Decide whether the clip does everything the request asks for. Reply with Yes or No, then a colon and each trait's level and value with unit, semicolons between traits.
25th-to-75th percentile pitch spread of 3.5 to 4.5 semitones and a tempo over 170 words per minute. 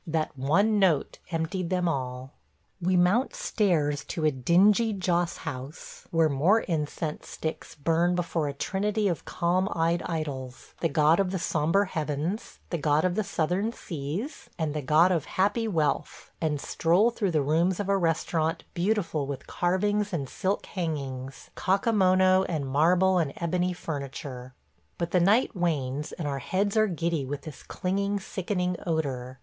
No: average, 4.0 semitones; average, 165 wpm